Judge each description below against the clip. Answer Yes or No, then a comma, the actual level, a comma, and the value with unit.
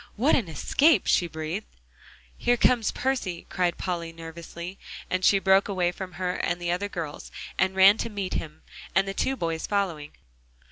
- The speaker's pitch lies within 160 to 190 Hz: Yes, medium, 185 Hz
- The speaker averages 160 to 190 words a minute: Yes, average, 175 wpm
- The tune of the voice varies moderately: Yes, average, 3.0 semitones